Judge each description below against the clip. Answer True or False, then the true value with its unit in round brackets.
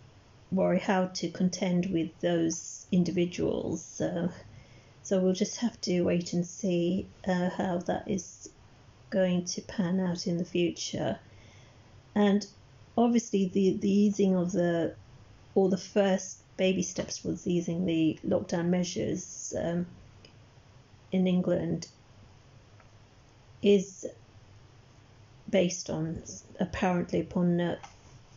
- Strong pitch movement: True (7.8 semitones)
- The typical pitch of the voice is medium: True (175 Hz)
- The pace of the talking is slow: True (110 wpm)